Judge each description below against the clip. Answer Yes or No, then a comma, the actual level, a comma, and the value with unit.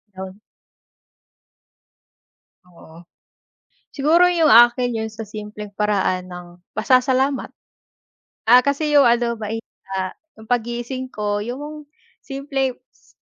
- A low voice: No, high, 235 Hz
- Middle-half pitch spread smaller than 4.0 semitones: No, average, 4.5 semitones